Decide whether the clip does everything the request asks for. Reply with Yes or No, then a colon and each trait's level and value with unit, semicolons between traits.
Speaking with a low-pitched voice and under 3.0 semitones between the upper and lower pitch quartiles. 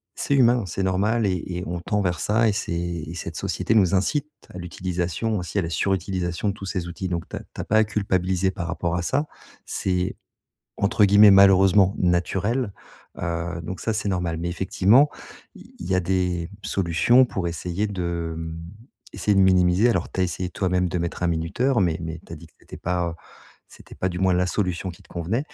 Yes: very low, 90 Hz; narrow, 2.6 semitones